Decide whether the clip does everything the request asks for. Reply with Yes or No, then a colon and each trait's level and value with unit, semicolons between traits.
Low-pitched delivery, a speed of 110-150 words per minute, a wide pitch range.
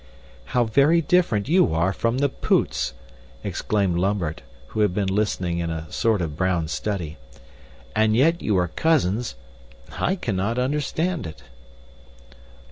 Yes: low, 105 Hz; slow, 135 wpm; wide, 6.9 semitones